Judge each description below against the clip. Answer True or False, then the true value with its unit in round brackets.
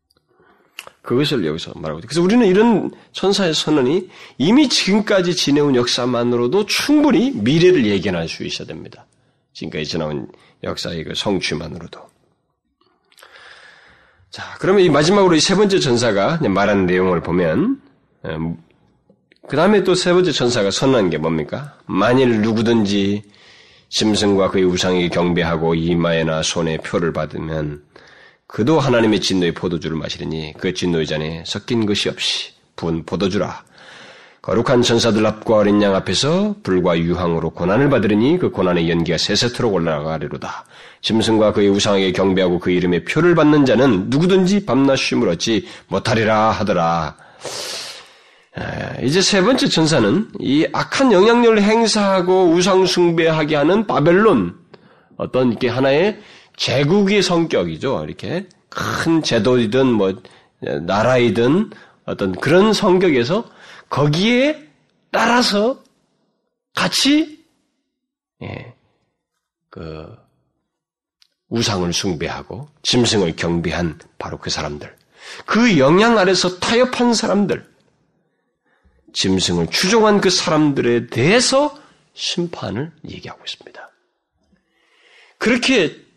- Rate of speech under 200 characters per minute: False (275 characters per minute)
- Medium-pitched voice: False (125 Hz)